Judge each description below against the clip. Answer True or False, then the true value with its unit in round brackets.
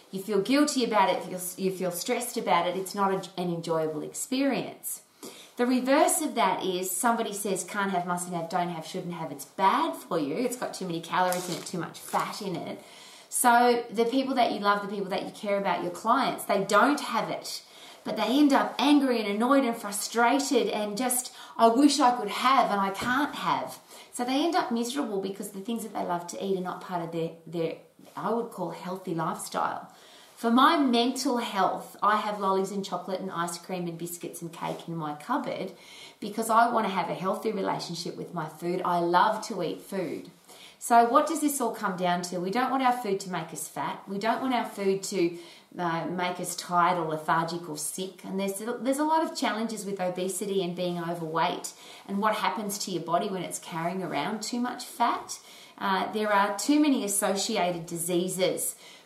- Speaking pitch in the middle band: False (200 Hz)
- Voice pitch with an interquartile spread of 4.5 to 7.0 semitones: True (5.1 semitones)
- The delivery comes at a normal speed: False (210 wpm)